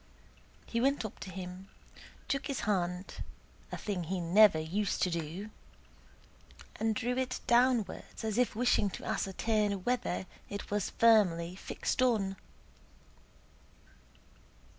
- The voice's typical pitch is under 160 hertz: No, high, 205 Hz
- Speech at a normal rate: No, slow, 120 wpm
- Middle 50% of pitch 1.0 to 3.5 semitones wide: No, average, 4.1 semitones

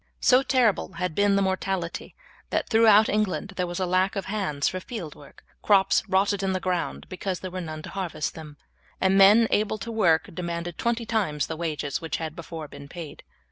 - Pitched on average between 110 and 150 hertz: No, medium, 185 Hz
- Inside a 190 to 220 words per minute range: Yes, average, 200 wpm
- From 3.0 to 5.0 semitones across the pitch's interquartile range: Yes, average, 3.7 semitones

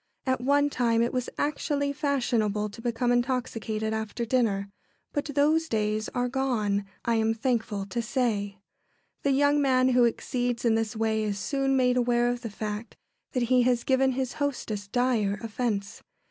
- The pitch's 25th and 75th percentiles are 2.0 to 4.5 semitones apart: Yes, average, 3.1 semitones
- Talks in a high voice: Yes, high, 240 Hz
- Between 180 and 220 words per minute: No, average, 165 wpm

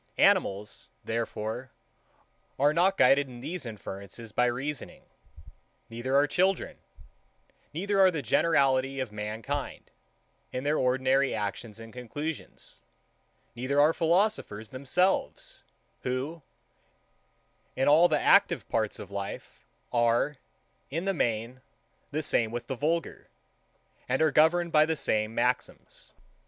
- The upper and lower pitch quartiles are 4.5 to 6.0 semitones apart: Yes, average, 5.2 semitones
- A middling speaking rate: No, slow, 120 wpm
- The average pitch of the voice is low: Yes, low, 130 Hz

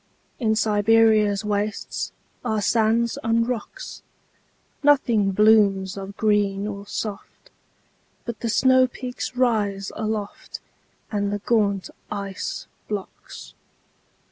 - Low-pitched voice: No, high, 215 Hz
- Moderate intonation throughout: No, narrow, 2.0 semitones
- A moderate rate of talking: No, slow, 80 wpm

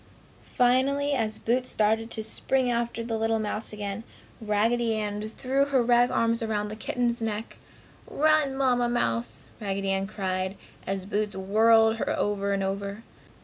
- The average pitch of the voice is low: No, high, 220 Hz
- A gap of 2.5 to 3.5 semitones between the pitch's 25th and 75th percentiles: Yes, average, 2.9 semitones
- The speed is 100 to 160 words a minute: Yes, average, 150 wpm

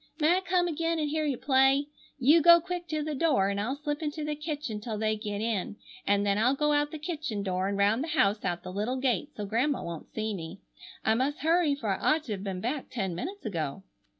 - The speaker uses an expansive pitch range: Yes, wide, 6.9 semitones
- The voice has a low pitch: No, very high, 260 Hz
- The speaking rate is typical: No, fast, 245 wpm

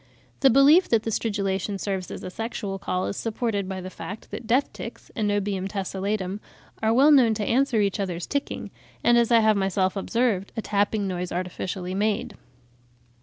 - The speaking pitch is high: Yes, high, 205 Hz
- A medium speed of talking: Yes, average, 175 wpm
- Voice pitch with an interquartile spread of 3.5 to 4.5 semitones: No, average, 3.1 semitones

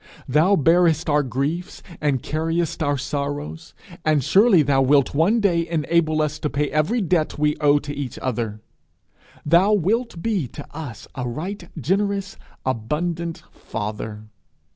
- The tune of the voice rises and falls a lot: No, average, 3.5 semitones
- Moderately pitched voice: Yes, medium, 155 Hz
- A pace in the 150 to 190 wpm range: No, average, 140 wpm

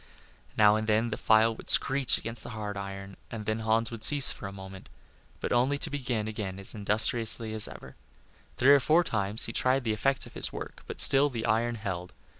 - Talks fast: Yes, fast, 210 wpm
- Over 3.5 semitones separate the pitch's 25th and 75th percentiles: No, narrow, 2.6 semitones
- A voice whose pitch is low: Yes, low, 110 Hz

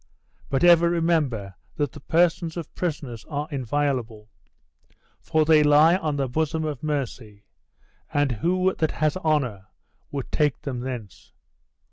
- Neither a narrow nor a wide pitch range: Yes, average, 4.2 semitones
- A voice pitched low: No, medium, 145 Hz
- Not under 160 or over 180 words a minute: No, slow, 135 wpm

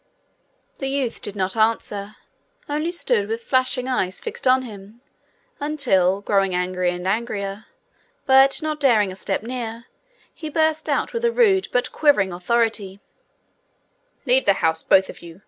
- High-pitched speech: Yes, high, 225 Hz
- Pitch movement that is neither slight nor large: No, wide, 5.7 semitones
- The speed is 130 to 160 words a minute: Yes, average, 150 wpm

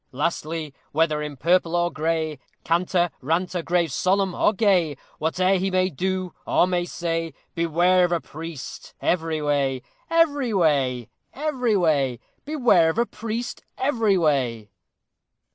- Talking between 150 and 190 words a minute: No, slow, 135 wpm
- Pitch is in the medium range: Yes, medium, 170 Hz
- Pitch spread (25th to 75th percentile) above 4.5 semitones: No, average, 3.5 semitones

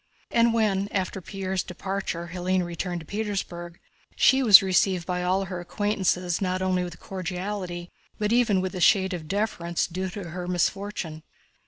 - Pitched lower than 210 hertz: Yes, medium, 185 Hz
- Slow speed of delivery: No, average, 155 wpm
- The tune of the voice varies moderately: No, narrow, 2.1 semitones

